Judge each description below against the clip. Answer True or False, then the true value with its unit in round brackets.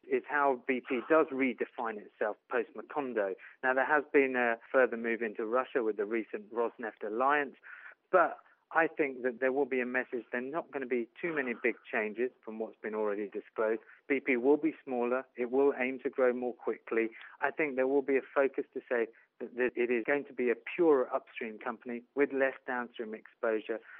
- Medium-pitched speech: False (130 Hz)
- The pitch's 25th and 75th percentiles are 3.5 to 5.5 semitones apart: False (2.8 semitones)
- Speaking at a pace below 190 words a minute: False (200 wpm)